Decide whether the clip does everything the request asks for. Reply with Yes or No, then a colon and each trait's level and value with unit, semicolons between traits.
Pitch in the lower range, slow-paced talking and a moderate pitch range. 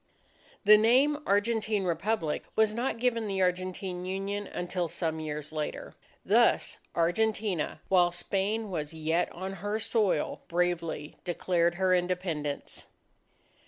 No: medium, 185 Hz; slow, 120 wpm; average, 3.7 semitones